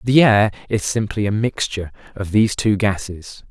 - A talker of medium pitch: No, low, 105 Hz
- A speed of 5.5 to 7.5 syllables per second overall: No, 5.1 syllables/s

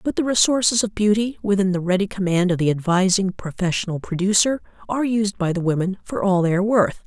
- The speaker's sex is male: No, female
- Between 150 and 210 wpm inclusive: Yes, fast, 205 wpm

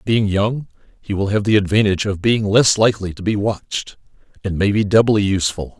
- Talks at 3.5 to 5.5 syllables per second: No, 5.7 syllables/s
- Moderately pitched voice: No, low, 100 Hz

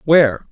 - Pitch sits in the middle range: Yes, medium, 145 Hz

